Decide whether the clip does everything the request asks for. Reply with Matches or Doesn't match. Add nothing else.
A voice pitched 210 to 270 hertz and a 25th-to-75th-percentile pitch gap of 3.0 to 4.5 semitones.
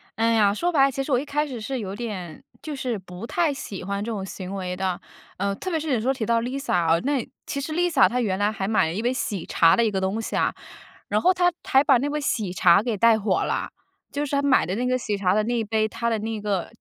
Doesn't match